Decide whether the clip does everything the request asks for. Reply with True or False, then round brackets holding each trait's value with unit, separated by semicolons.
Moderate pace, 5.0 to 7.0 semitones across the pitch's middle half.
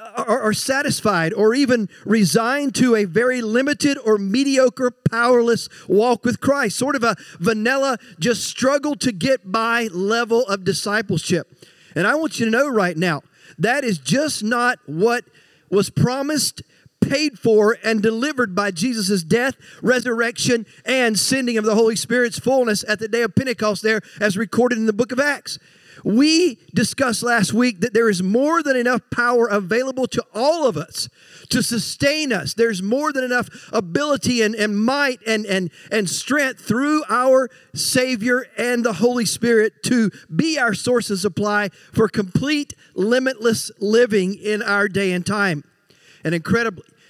False (160 wpm; 3.4 semitones)